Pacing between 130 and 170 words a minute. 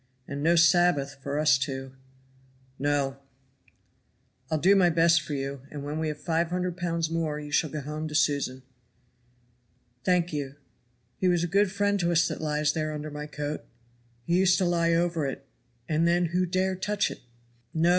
No: average, 185 wpm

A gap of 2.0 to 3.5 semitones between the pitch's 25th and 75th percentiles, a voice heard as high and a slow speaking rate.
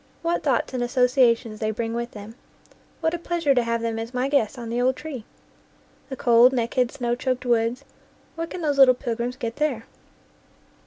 No: average, 2.8 semitones; high, 245 Hz; average, 195 wpm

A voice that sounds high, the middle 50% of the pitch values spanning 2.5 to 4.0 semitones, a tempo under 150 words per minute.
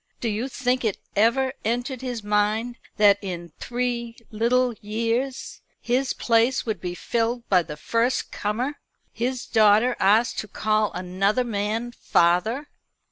Yes: high, 230 Hz; average, 3.0 semitones; slow, 135 wpm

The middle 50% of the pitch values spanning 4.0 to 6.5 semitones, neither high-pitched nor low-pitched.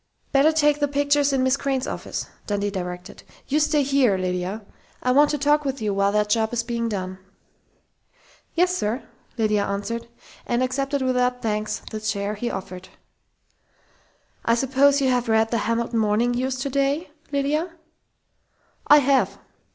No: average, 4.8 semitones; high, 245 Hz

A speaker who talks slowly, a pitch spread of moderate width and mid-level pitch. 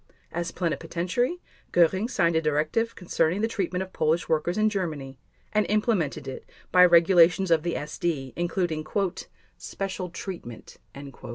Yes: slow, 130 wpm; average, 3.2 semitones; medium, 175 Hz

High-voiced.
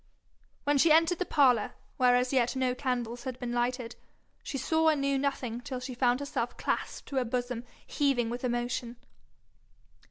Yes: very high, 255 Hz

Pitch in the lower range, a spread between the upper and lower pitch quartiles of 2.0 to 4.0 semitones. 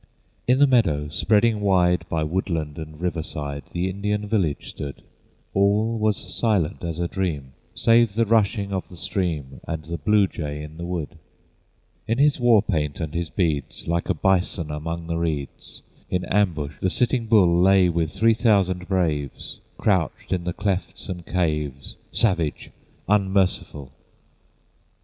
No: very low, 90 Hz; average, 4.5 semitones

